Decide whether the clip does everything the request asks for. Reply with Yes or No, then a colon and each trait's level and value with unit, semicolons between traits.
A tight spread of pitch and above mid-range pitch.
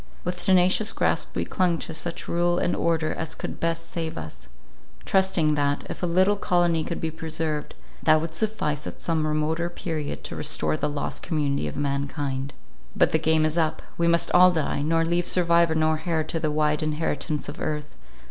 No: narrow, 2.0 semitones; medium, 160 Hz